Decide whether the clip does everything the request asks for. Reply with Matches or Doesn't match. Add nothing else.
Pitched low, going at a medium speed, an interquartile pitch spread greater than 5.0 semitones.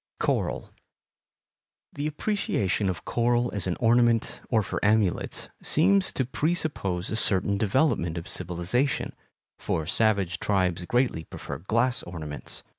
Doesn't match